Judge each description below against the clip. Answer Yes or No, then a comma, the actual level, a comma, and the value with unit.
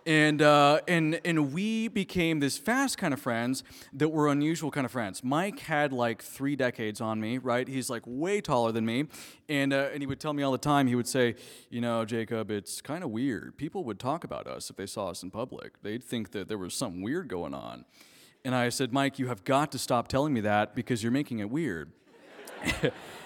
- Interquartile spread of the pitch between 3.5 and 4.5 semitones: Yes, average, 3.8 semitones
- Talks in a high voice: No, low, 130 Hz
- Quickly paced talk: Yes, fast, 225 wpm